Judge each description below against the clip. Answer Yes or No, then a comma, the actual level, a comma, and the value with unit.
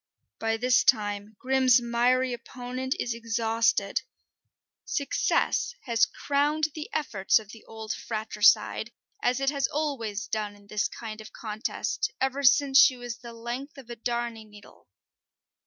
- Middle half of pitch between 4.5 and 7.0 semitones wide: No, average, 3.0 semitones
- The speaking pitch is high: Yes, high, 235 Hz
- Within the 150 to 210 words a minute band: No, average, 140 wpm